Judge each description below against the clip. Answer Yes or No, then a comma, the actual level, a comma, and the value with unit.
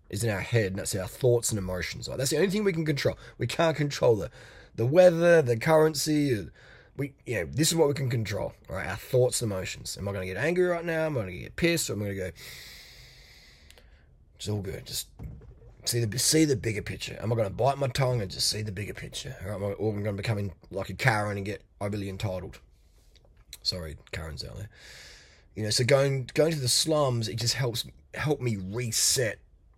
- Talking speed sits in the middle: No, fast, 235 wpm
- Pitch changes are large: Yes, wide, 5.7 semitones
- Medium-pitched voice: No, low, 115 Hz